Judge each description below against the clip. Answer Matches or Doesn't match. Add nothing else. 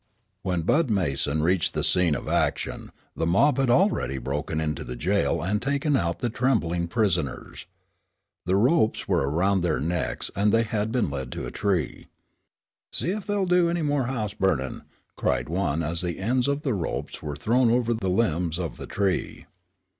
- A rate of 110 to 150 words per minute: Doesn't match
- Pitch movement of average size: Doesn't match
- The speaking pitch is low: Matches